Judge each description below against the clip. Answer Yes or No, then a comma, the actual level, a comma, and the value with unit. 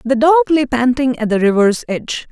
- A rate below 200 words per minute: No, fast, 205 wpm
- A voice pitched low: No, very high, 255 Hz